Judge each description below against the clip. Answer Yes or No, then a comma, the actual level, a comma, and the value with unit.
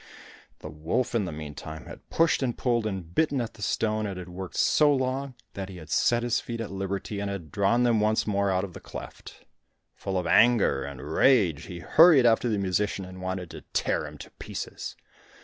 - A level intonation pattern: No, average, 4.5 semitones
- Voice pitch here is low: Yes, low, 100 Hz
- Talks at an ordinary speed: No, fast, 210 wpm